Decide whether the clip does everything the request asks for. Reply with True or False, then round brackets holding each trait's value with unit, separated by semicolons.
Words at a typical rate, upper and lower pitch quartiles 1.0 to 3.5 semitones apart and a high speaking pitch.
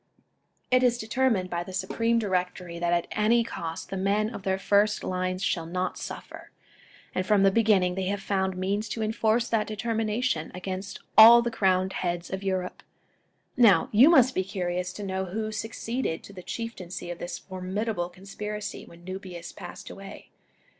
True (170 wpm; 3.1 semitones; 195 Hz)